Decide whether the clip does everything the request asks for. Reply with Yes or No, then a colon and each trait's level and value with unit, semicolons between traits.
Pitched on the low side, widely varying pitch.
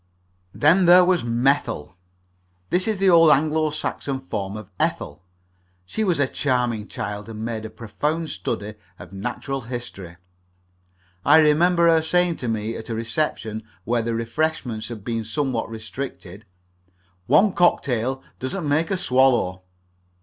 Yes: low, 125 Hz; wide, 6.1 semitones